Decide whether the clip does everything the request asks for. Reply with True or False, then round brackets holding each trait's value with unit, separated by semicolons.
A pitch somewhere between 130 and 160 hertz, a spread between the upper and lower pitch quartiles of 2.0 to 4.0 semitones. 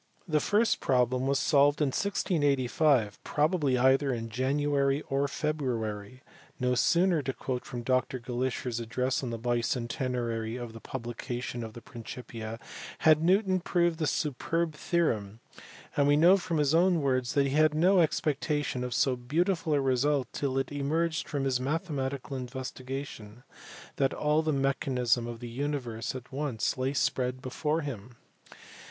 True (135 Hz; 3.5 semitones)